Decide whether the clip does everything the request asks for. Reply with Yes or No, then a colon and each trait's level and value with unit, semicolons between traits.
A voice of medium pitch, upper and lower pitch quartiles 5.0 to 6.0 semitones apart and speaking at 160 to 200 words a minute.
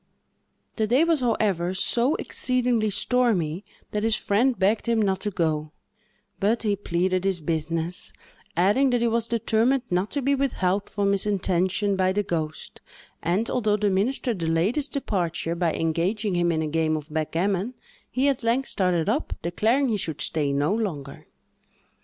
No: high, 200 Hz; average, 5.3 semitones; average, 165 wpm